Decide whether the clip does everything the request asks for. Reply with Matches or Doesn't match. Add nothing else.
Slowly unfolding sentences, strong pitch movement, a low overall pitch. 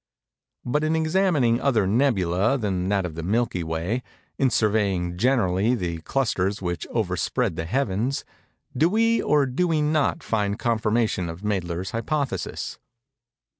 Matches